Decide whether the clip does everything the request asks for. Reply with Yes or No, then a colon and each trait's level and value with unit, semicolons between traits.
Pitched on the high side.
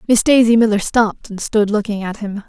Yes: high, 215 Hz